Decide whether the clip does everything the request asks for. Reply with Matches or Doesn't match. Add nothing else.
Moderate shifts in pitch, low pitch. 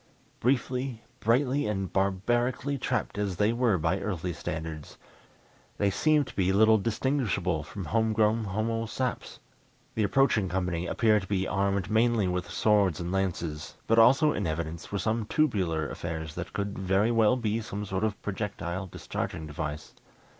Matches